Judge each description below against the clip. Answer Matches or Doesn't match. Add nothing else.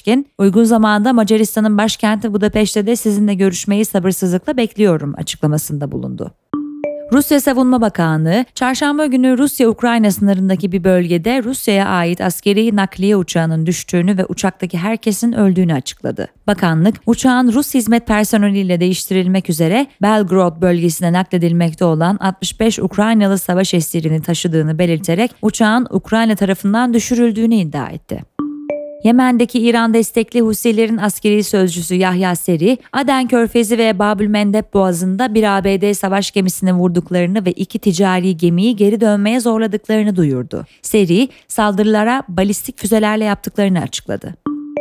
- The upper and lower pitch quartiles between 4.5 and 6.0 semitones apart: Doesn't match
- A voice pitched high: Matches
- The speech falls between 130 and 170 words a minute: Doesn't match